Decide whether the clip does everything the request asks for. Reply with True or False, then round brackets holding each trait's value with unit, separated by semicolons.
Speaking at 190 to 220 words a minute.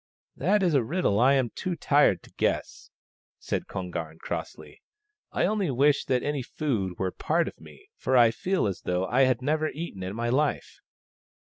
True (200 wpm)